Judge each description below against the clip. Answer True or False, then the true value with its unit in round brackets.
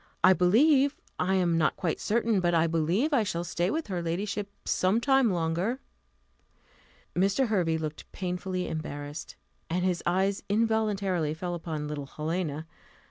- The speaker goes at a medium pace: True (145 wpm)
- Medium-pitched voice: True (180 Hz)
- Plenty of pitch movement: False (4.2 semitones)